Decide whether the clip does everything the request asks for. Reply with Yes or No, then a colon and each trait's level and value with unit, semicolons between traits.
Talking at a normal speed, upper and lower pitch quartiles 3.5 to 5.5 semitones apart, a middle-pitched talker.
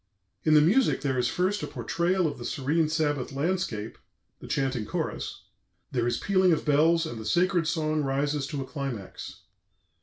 Yes: average, 180 wpm; average, 4.1 semitones; medium, 150 Hz